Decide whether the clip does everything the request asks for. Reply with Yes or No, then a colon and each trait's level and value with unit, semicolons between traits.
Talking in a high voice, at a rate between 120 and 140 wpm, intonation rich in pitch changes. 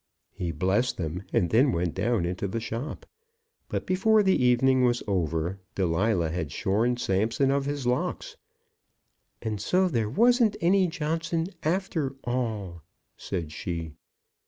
No: low, 115 Hz; slow, 135 wpm; wide, 8.2 semitones